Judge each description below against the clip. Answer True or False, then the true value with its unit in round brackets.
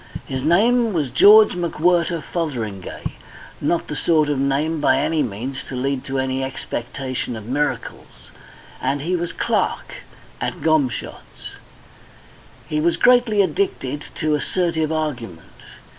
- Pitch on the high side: False (150 Hz)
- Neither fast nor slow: False (130 wpm)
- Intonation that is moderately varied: True (4.5 semitones)